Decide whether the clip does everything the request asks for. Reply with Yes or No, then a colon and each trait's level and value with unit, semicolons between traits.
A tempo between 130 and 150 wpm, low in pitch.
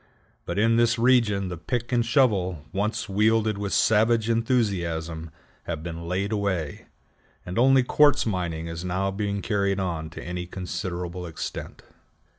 Yes: average, 145 wpm; low, 100 Hz